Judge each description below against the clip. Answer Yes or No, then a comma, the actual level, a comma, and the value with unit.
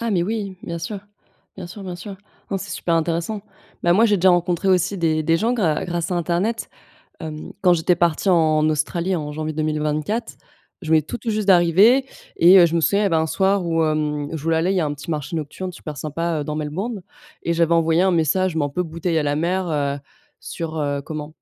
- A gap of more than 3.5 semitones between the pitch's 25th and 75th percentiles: No, average, 3.2 semitones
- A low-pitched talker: No, medium, 170 Hz